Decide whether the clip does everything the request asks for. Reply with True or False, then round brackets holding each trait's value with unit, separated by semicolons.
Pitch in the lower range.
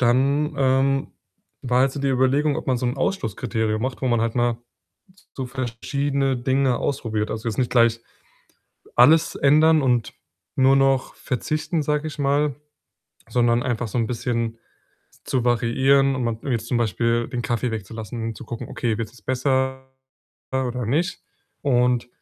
True (125 Hz)